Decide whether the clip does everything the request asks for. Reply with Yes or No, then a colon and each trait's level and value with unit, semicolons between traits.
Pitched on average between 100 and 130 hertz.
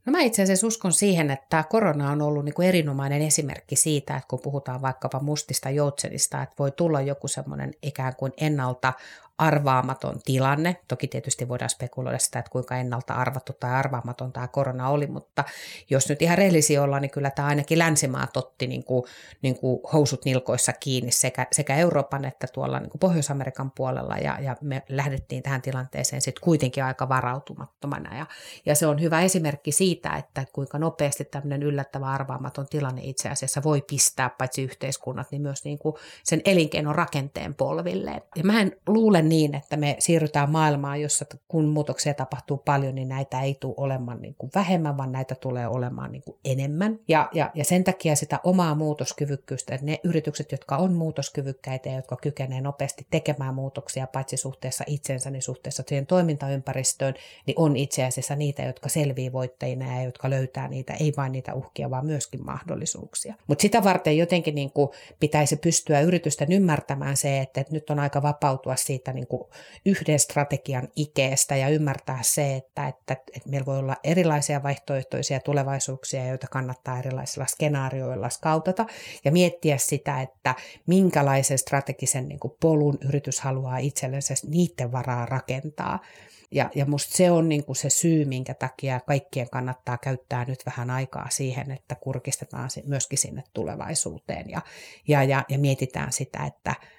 No: medium, 140 Hz